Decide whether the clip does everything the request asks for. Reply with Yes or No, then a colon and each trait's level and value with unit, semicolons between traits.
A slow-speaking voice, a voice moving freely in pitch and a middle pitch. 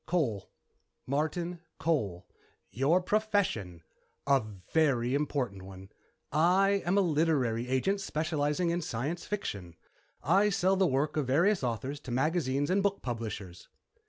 Yes: slow, 130 wpm; wide, 6.6 semitones; medium, 150 Hz